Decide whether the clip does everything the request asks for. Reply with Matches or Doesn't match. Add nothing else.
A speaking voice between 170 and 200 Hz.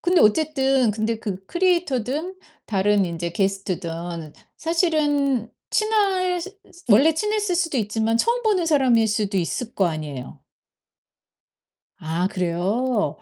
Doesn't match